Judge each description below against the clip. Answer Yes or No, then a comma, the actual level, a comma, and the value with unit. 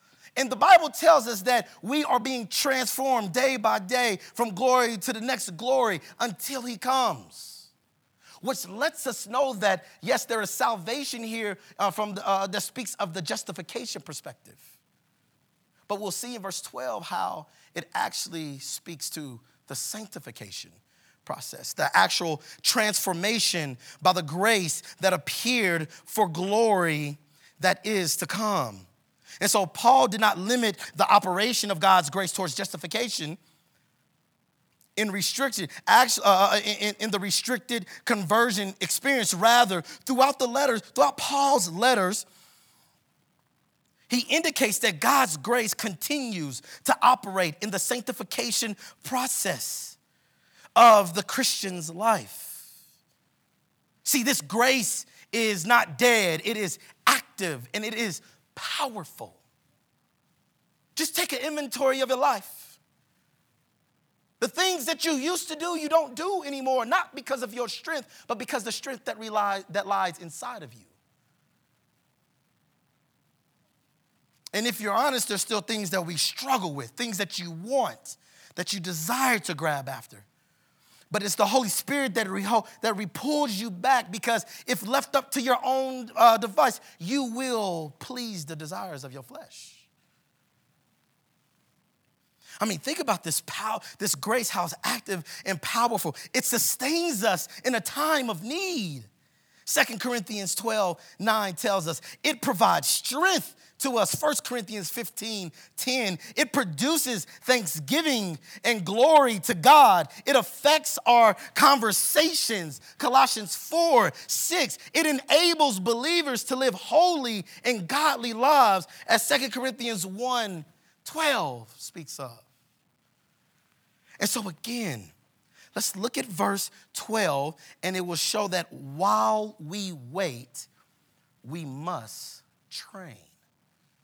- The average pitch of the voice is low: No, high, 215 Hz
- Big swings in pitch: Yes, wide, 5.8 semitones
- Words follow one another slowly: Yes, slow, 130 wpm